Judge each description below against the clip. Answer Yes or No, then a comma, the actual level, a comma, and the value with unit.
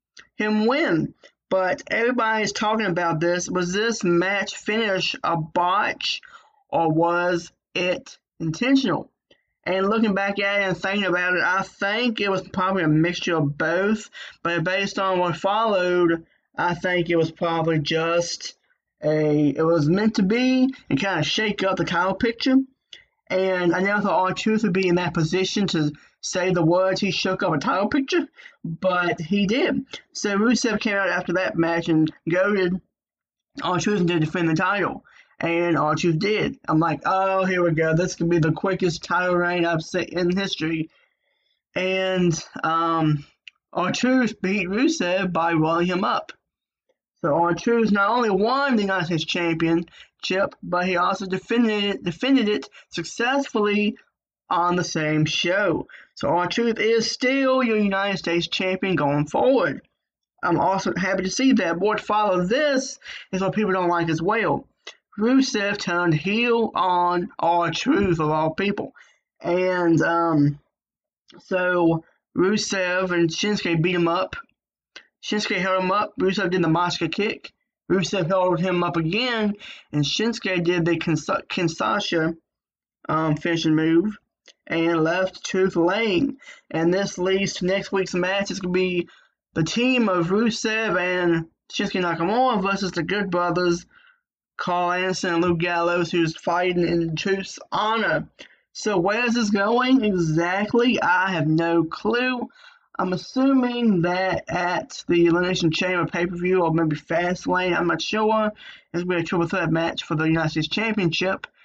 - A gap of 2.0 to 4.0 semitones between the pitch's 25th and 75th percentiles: Yes, average, 3.7 semitones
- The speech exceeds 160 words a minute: No, average, 155 wpm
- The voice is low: No, medium, 185 Hz